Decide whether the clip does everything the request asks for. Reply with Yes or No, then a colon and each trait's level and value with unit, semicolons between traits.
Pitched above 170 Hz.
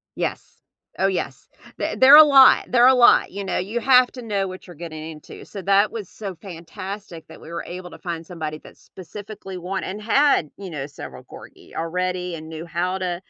Yes: medium, 185 Hz